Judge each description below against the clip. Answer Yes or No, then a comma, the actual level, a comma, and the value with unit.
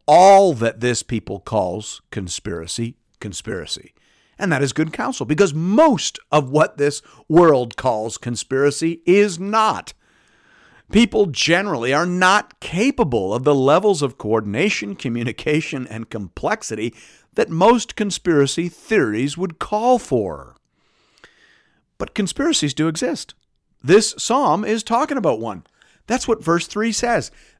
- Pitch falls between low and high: Yes, medium, 160 Hz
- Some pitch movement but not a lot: No, wide, 9.0 semitones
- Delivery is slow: Yes, slow, 125 wpm